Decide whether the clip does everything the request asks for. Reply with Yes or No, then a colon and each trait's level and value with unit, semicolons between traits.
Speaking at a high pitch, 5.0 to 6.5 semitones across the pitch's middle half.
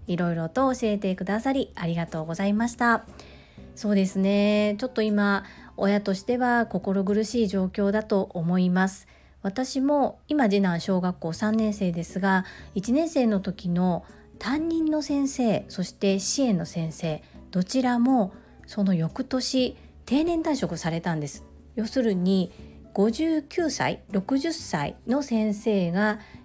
Yes: high, 205 Hz; average, 5.3 semitones